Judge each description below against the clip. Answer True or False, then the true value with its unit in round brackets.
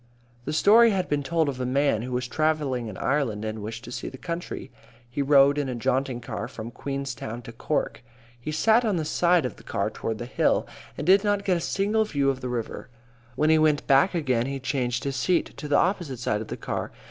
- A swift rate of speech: True (230 wpm)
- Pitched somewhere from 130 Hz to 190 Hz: True (140 Hz)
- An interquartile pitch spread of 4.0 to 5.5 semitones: True (4.8 semitones)